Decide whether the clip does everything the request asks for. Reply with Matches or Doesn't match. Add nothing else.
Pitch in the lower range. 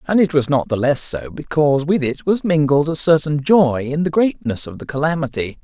Doesn't match